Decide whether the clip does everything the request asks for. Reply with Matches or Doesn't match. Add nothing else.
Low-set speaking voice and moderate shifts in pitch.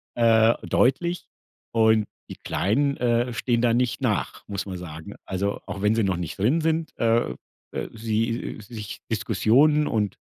Matches